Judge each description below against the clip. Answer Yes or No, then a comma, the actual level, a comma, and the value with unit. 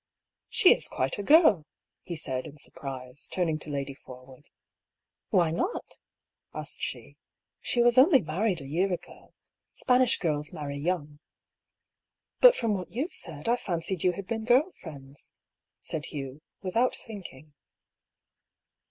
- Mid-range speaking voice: Yes, medium, 170 Hz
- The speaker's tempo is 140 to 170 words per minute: Yes, average, 150 wpm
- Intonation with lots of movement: Yes, wide, 7.3 semitones